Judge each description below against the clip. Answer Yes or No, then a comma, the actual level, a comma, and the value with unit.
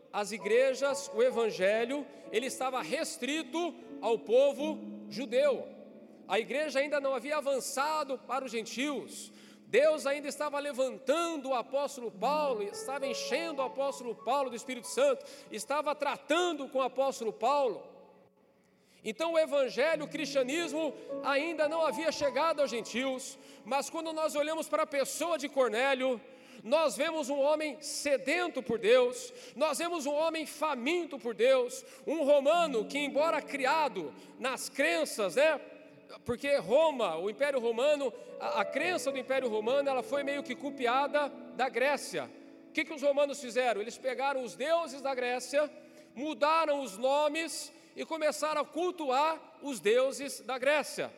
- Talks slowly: No, average, 145 wpm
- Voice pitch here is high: Yes, very high, 280 Hz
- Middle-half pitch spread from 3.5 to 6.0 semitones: No, average, 2.9 semitones